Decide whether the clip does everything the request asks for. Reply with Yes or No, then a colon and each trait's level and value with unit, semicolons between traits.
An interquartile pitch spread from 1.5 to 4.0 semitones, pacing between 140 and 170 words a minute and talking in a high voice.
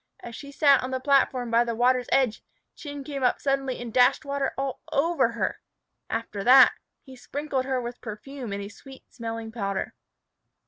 No: average, 2.9 semitones; average, 180 wpm; very high, 255 Hz